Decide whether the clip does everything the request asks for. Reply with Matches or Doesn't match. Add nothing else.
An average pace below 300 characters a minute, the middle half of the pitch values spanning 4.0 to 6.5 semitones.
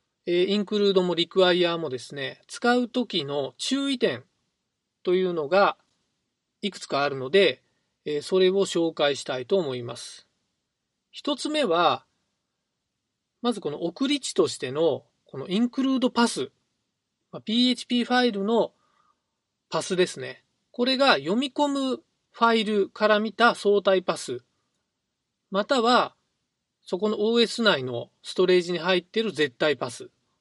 Matches